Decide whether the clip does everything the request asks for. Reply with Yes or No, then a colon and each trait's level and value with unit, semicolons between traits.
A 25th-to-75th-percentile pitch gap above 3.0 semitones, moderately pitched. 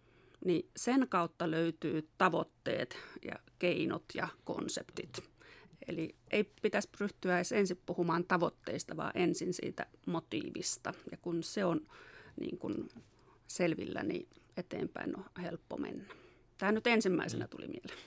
Yes: average, 3.8 semitones; medium, 180 Hz